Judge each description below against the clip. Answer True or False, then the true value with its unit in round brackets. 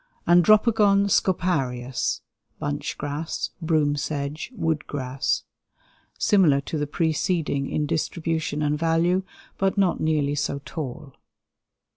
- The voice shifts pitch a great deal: False (3.4 semitones)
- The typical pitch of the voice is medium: True (155 Hz)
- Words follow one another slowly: True (105 wpm)